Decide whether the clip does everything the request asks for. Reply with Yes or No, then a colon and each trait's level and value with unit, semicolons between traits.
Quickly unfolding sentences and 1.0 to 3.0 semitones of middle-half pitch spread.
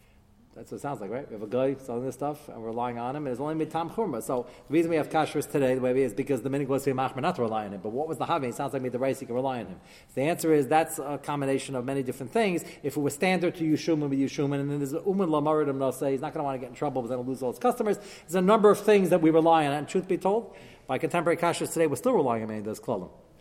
No: fast, 335 wpm; average, 4.0 semitones